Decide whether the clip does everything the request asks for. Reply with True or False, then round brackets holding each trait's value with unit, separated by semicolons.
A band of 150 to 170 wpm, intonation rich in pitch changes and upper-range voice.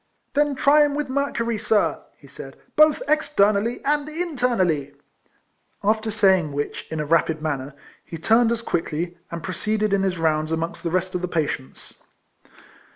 True (160 wpm; 7.3 semitones; 200 Hz)